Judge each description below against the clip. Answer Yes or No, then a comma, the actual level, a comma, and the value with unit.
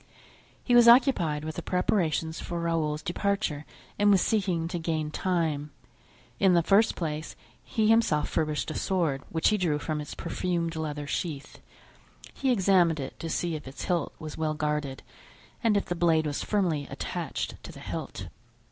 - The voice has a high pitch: No, medium, 165 Hz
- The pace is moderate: Yes, average, 170 wpm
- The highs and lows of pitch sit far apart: No, average, 3.7 semitones